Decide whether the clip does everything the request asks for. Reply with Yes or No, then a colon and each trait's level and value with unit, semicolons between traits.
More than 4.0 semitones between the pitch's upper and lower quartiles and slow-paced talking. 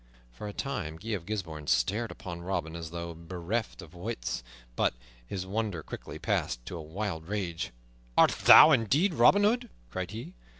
No: average, 5.0 semitones; average, 170 wpm